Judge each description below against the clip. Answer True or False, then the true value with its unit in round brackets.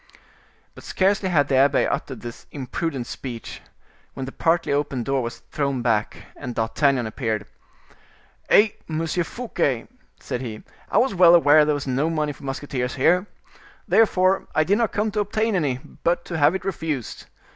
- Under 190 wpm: True (170 wpm)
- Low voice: False (145 Hz)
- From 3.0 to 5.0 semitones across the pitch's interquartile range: False (5.4 semitones)